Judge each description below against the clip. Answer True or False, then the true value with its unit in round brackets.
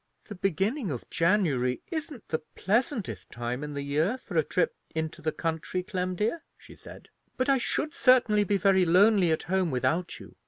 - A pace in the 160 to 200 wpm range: True (185 wpm)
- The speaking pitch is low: False (185 Hz)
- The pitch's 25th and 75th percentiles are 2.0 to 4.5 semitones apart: False (5.1 semitones)